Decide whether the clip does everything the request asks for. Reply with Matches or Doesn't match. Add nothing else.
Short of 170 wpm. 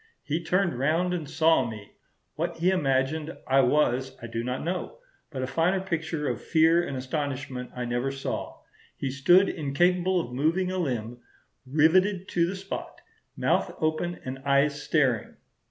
Matches